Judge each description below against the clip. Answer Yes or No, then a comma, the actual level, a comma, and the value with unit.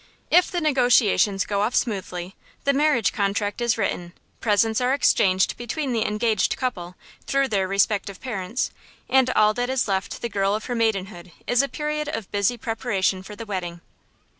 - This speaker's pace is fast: No, average, 170 wpm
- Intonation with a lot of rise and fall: No, average, 4.1 semitones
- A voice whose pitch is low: No, high, 220 Hz